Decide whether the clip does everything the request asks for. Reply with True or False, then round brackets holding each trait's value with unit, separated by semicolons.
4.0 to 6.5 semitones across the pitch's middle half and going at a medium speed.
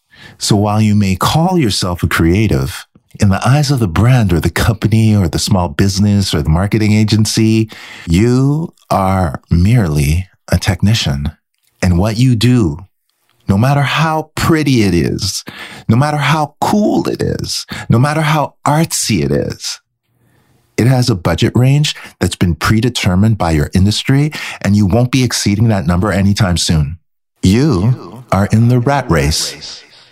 True (4.5 semitones; 155 wpm)